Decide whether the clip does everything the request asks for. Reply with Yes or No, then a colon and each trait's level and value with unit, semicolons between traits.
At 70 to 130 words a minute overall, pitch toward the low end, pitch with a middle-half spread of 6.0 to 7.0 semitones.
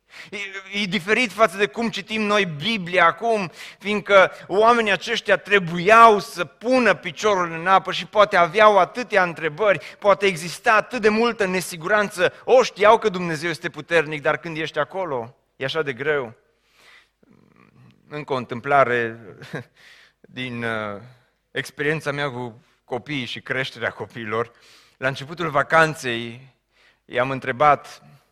No: average, 125 wpm; medium, 175 Hz; wide, 6.7 semitones